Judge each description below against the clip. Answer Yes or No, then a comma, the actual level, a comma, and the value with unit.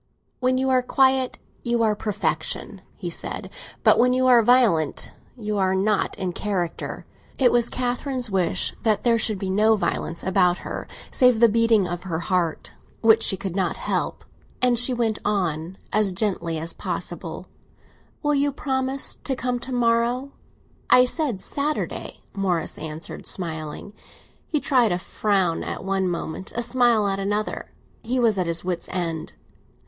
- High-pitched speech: Yes, high, 215 Hz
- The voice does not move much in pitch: No, average, 5.0 semitones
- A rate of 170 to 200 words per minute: No, average, 160 wpm